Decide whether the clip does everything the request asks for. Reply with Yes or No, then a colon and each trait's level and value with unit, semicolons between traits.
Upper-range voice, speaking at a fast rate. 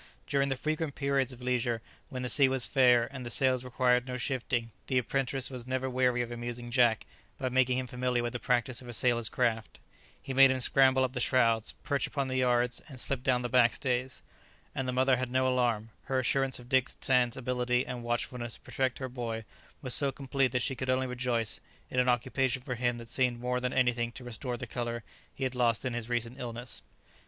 No: low, 125 Hz; fast, 220 wpm